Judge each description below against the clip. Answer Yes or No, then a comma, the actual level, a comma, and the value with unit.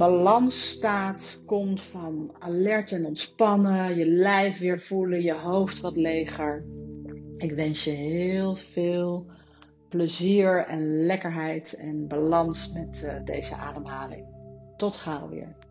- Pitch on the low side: No, medium, 175 Hz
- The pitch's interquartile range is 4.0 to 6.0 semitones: No, average, 3.6 semitones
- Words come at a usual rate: No, slow, 120 wpm